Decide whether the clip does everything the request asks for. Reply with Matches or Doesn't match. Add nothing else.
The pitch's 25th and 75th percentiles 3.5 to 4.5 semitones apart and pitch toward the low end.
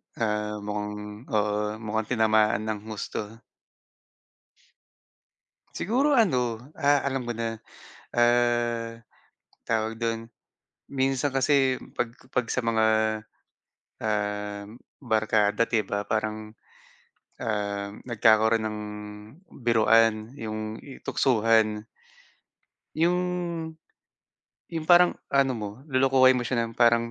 Doesn't match